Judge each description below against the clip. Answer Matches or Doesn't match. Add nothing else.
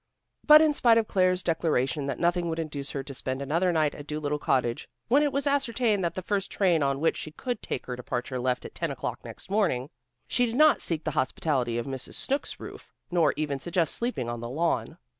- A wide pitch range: Matches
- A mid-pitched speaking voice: Matches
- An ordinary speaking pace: Doesn't match